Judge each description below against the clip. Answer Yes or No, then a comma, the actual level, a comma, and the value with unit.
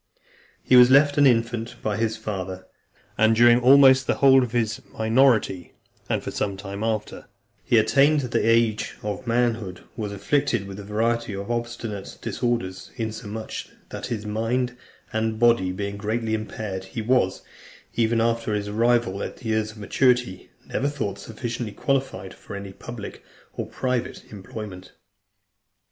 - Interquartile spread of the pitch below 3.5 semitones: Yes, average, 2.8 semitones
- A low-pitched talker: Yes, low, 110 Hz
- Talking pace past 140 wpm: Yes, average, 150 wpm